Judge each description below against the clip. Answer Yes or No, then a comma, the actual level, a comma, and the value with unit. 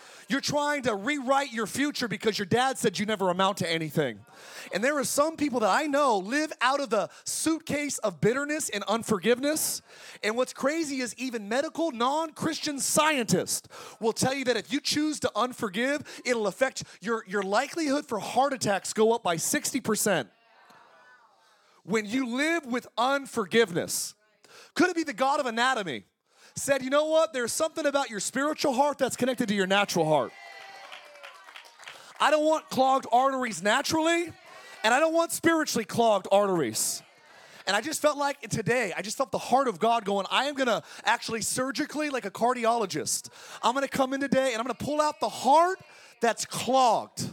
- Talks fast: No, average, 175 wpm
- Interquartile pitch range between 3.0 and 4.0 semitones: No, average, 4.8 semitones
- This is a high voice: Yes, very high, 255 Hz